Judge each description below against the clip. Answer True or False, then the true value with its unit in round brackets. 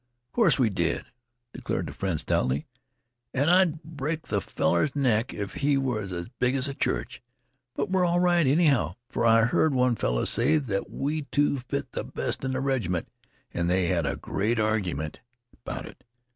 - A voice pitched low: True (125 Hz)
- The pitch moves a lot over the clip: True (7.2 semitones)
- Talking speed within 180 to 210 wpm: True (185 wpm)